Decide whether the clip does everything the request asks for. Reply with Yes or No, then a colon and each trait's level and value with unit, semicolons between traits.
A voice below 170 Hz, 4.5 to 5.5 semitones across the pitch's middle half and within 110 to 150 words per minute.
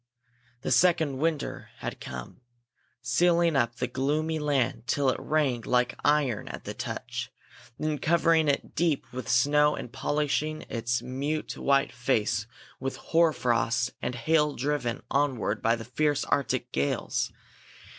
No: medium, 140 Hz; average, 4.0 semitones; average, 140 wpm